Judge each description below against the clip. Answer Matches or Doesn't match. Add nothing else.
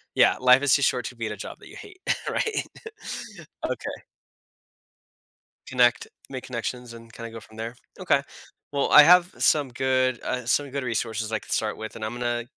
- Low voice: Matches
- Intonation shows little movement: Doesn't match